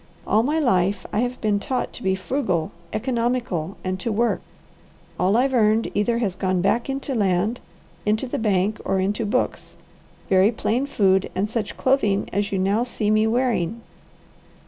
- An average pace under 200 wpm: Yes, average, 170 wpm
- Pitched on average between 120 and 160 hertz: No, high, 215 Hz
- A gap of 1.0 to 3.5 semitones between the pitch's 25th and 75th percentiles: No, average, 3.9 semitones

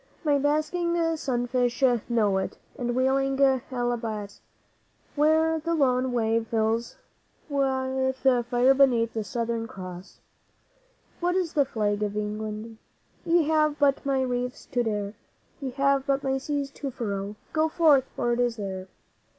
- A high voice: Yes, very high, 255 Hz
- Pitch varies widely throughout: No, average, 3.8 semitones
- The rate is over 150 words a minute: No, average, 140 wpm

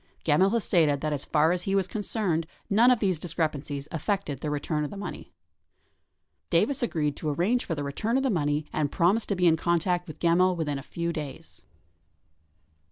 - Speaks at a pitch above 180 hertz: No, medium, 170 Hz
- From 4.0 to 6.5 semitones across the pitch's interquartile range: Yes, average, 4.5 semitones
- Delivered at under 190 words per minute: No, average, 195 wpm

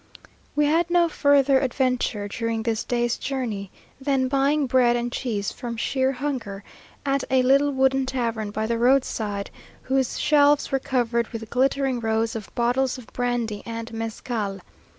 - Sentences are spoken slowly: No, average, 155 wpm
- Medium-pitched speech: No, very high, 250 Hz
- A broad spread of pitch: No, average, 3.0 semitones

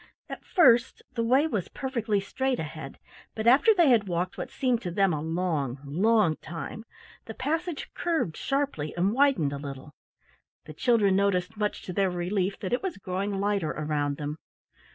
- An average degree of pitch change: No, wide, 6.9 semitones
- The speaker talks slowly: No, average, 175 wpm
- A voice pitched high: Yes, high, 200 Hz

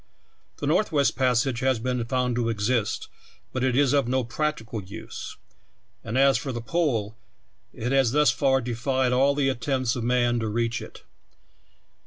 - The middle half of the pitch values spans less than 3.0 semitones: Yes, narrow, 2.6 semitones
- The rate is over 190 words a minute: No, average, 165 wpm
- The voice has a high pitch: No, low, 125 Hz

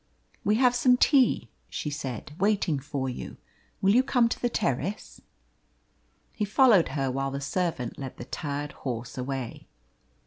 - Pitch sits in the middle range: Yes, medium, 150 Hz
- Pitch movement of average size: No, wide, 8.0 semitones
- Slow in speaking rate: No, average, 150 wpm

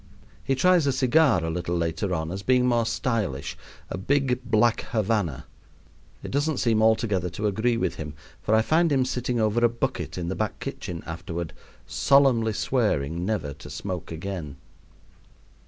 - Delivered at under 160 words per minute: No, average, 165 wpm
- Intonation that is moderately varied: No, wide, 6.3 semitones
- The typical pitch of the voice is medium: No, low, 110 Hz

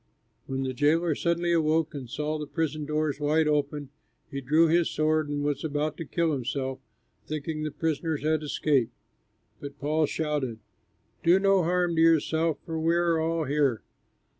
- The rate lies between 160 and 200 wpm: Yes, average, 165 wpm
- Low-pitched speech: No, medium, 155 Hz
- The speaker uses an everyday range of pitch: No, narrow, 2.1 semitones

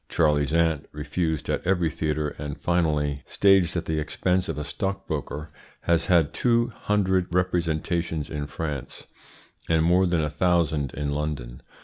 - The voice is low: Yes, very low, 80 Hz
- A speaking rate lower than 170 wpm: Yes, average, 145 wpm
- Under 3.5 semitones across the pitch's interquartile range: Yes, average, 3.0 semitones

